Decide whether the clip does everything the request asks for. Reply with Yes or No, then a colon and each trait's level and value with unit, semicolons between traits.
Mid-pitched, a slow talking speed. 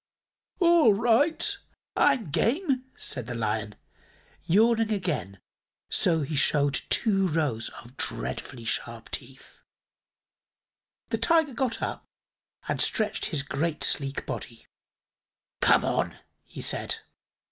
Yes: medium, 165 Hz; slow, 115 wpm